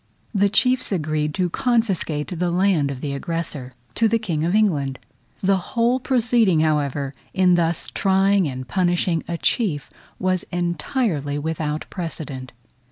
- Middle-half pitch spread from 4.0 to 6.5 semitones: Yes, average, 4.8 semitones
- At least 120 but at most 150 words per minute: Yes, average, 140 wpm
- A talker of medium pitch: Yes, medium, 175 Hz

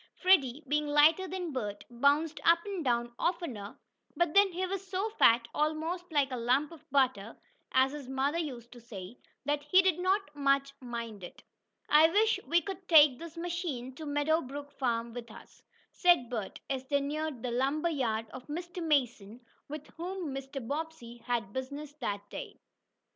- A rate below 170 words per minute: No, average, 175 wpm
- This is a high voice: Yes, very high, 285 Hz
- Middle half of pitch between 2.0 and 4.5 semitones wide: No, average, 5.3 semitones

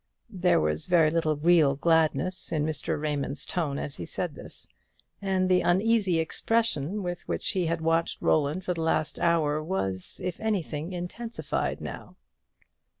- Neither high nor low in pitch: Yes, medium, 165 Hz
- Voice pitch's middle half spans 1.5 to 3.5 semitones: Yes, average, 3.2 semitones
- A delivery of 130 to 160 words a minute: Yes, average, 150 wpm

